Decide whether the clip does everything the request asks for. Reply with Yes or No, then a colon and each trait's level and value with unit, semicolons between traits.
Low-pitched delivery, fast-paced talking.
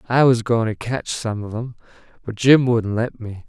Yes: low, 115 Hz; fast, 225 wpm